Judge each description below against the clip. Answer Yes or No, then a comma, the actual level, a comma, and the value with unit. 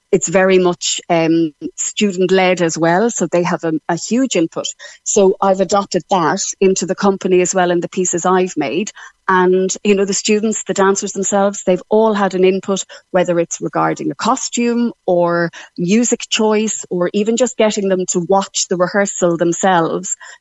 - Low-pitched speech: No, high, 190 Hz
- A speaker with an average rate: Yes, average, 175 wpm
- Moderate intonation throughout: No, narrow, 2.1 semitones